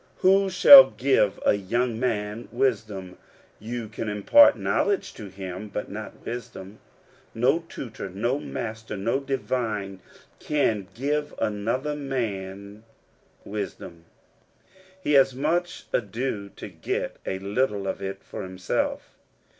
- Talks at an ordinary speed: No, slow, 115 wpm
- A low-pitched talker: Yes, low, 110 Hz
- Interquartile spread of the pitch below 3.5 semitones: No, average, 5.0 semitones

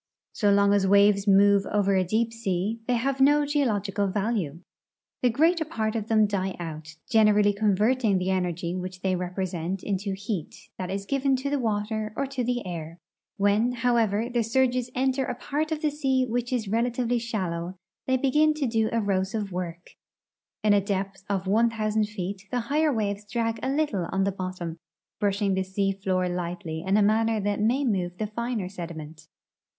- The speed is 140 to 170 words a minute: No, average, 180 wpm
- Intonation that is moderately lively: Yes, average, 4.0 semitones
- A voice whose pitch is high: Yes, high, 205 Hz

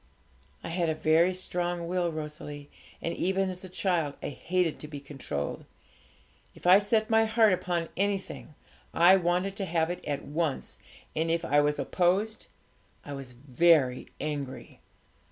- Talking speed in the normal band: Yes, average, 155 wpm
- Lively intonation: No, average, 3.8 semitones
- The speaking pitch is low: No, medium, 170 Hz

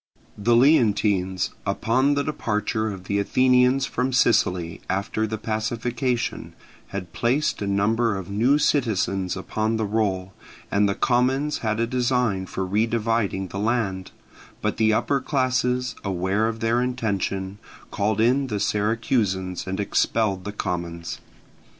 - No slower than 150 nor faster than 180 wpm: No, slow, 135 wpm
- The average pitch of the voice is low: Yes, low, 110 Hz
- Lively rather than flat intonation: No, average, 3.9 semitones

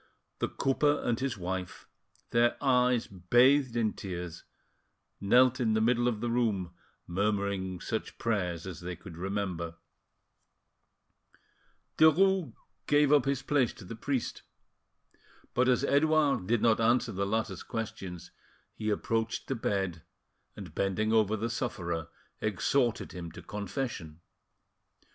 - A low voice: Yes, low, 110 Hz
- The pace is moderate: No, slow, 130 wpm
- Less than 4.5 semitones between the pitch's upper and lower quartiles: No, average, 4.9 semitones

